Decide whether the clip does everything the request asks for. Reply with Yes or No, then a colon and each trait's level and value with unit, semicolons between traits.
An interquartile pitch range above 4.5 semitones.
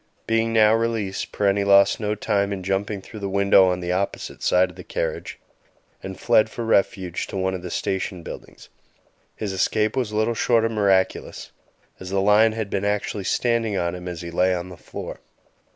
No: narrow, 2.6 semitones